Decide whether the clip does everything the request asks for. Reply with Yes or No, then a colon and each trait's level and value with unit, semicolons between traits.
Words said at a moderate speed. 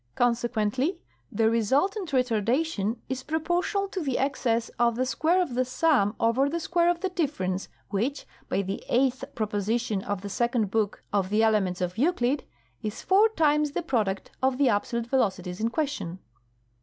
Yes: average, 165 wpm